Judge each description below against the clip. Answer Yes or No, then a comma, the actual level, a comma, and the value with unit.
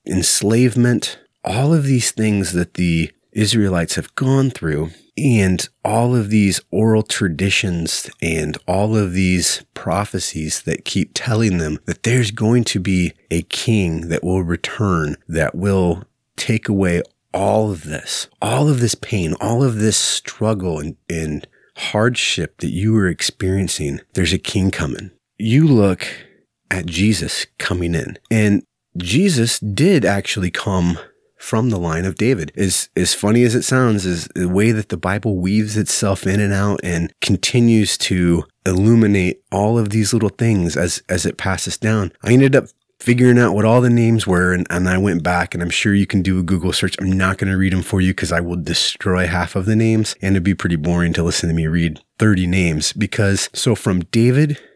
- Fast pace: No, average, 180 wpm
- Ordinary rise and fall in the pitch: Yes, average, 4.0 semitones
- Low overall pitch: Yes, very low, 95 Hz